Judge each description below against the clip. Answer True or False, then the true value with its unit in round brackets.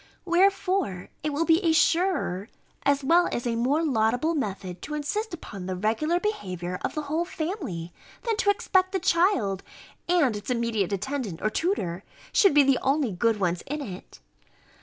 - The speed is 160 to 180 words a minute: True (170 wpm)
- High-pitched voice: True (280 Hz)